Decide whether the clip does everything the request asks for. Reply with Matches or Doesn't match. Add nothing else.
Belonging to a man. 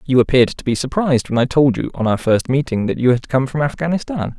Matches